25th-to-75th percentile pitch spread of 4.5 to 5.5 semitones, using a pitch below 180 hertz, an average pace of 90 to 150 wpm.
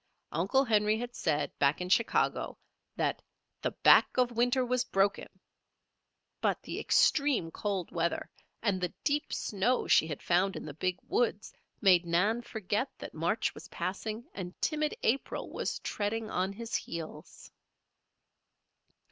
No: average, 4.9 semitones; high, 205 Hz; average, 140 wpm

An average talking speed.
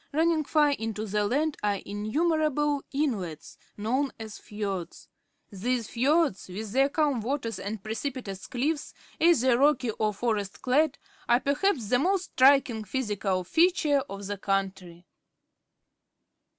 No: slow, 125 wpm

